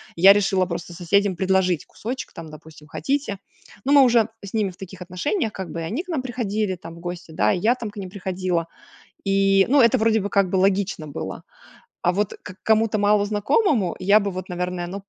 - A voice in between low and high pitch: No, high, 195 Hz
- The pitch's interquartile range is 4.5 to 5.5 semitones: No, average, 3.2 semitones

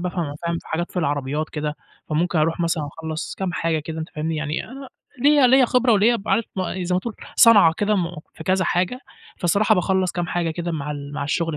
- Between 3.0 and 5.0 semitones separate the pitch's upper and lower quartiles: Yes, average, 4.0 semitones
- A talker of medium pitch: Yes, medium, 170 Hz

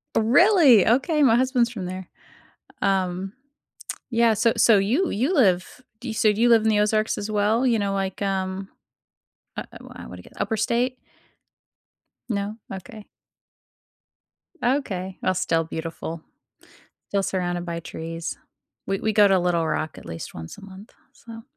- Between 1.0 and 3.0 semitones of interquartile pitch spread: No, average, 3.8 semitones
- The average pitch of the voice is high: Yes, high, 205 Hz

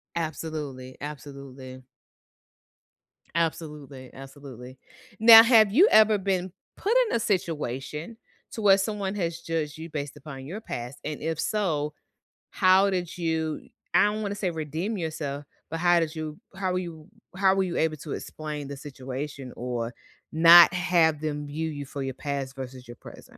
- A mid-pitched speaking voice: Yes, medium, 155 Hz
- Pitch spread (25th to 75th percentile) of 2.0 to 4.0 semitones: No, average, 4.5 semitones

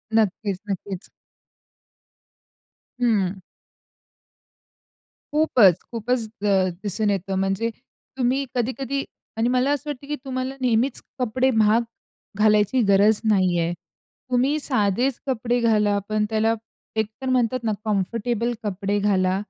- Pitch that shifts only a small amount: No, average, 3.8 semitones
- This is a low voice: No, high, 220 Hz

